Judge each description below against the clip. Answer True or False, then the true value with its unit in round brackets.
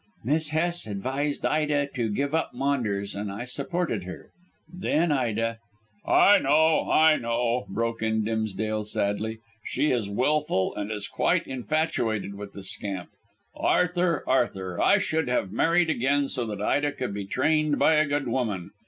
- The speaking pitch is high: False (125 Hz)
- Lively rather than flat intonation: True (6.3 semitones)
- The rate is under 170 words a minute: True (160 wpm)